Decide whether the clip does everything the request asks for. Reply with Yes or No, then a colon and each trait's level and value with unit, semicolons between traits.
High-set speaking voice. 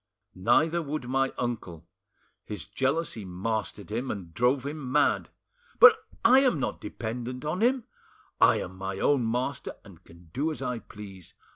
No: low, 125 Hz